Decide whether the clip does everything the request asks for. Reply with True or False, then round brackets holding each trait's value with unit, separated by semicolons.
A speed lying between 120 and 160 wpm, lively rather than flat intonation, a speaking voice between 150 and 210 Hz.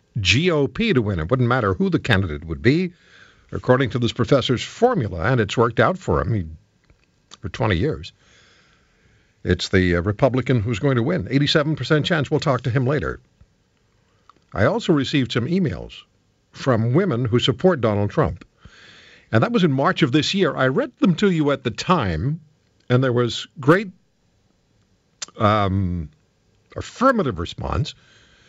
False (155 wpm; 5.8 semitones; 130 Hz)